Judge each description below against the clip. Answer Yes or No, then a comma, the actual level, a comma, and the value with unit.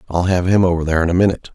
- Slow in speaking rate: No, fast, 310 wpm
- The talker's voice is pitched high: No, very low, 90 Hz